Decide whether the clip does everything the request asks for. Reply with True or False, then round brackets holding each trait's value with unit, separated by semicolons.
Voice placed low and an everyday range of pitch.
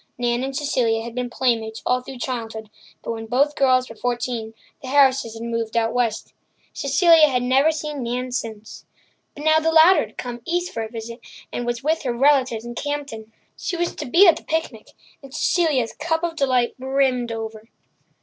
False (250 Hz; 3.9 semitones)